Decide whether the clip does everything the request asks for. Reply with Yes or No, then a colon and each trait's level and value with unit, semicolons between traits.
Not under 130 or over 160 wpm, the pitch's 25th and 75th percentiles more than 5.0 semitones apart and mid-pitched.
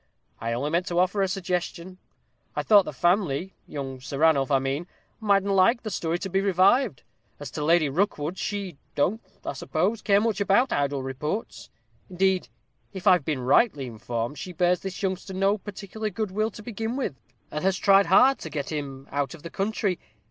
No: average, 190 wpm; wide, 5.4 semitones; medium, 180 Hz